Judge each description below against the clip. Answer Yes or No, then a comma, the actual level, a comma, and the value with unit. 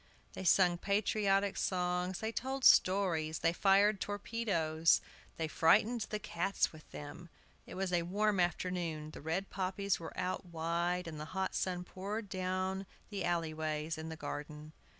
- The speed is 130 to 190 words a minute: Yes, average, 160 wpm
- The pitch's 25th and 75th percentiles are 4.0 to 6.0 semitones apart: No, average, 3.3 semitones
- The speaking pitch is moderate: Yes, medium, 180 Hz